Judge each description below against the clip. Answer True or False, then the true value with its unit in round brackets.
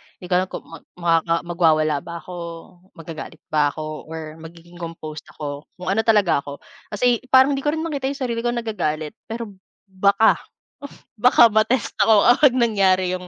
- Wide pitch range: True (6.2 semitones)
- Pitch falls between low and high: True (180 Hz)